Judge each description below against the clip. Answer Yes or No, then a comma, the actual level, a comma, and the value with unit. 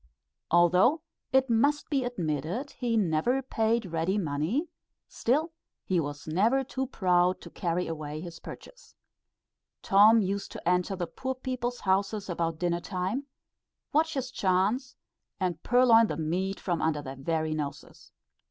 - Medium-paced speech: Yes, average, 145 wpm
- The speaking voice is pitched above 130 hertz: Yes, high, 190 Hz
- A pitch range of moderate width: No, wide, 6.8 semitones